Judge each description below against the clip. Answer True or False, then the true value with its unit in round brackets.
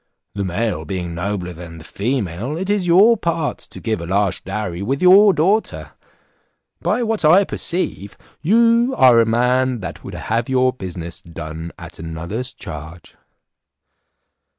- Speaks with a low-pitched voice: True (115 Hz)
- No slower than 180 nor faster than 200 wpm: False (150 wpm)